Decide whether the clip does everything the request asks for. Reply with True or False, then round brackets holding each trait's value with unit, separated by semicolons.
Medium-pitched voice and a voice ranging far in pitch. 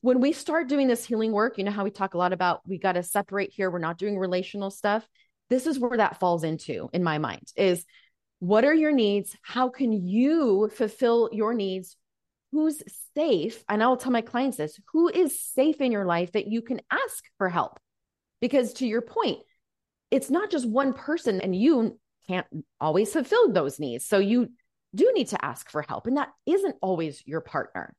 False (220 Hz; 6.1 semitones)